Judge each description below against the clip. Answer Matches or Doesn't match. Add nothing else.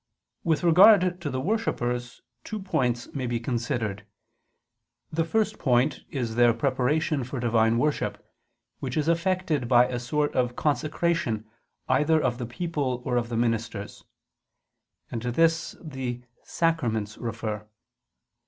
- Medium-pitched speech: Doesn't match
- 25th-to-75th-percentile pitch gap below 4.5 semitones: Doesn't match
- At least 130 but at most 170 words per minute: Matches